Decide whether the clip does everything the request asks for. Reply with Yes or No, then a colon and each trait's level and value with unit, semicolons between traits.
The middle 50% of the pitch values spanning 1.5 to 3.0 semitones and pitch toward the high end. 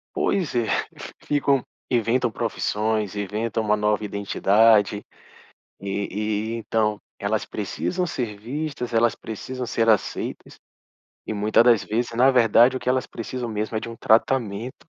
No: average, 2.7 semitones; low, 115 Hz